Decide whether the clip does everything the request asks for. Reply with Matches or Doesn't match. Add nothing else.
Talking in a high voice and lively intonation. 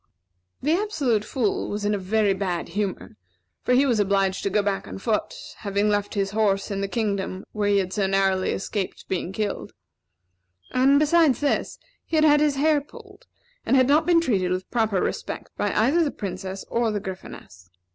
Matches